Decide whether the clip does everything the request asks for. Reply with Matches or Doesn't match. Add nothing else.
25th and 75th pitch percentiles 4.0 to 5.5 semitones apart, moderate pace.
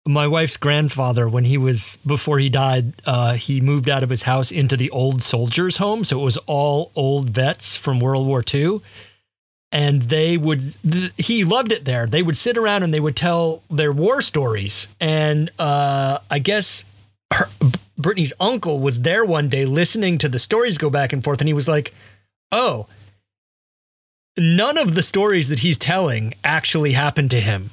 Matches